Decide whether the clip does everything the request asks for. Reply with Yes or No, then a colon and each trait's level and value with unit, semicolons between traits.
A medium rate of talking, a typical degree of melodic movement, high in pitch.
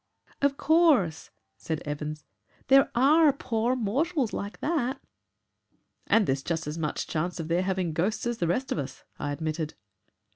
No: average, 155 wpm; wide, 9.0 semitones; high, 195 Hz